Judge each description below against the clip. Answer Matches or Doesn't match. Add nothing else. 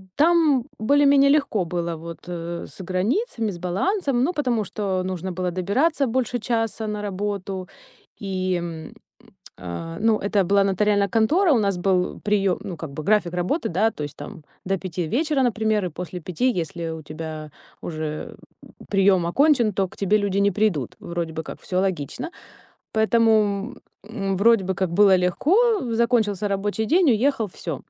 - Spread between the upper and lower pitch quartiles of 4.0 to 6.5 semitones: Matches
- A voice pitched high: Matches